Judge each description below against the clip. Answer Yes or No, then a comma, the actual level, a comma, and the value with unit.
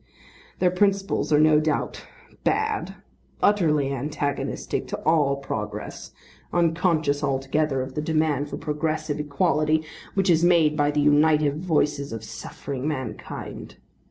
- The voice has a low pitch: No, medium, 150 Hz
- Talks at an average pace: No, slow, 125 wpm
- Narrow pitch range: Yes, narrow, 2.2 semitones